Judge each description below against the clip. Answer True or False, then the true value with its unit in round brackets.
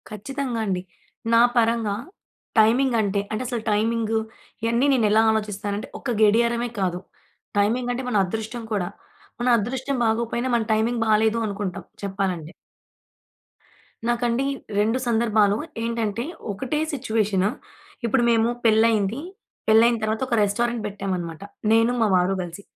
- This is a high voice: True (220 Hz)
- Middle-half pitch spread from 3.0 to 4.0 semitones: False (2.5 semitones)